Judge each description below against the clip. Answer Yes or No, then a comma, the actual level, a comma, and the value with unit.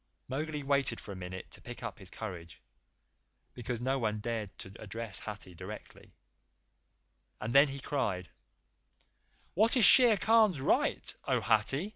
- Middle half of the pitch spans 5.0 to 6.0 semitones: Yes, wide, 5.4 semitones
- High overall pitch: No, low, 115 Hz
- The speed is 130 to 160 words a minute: Yes, average, 145 wpm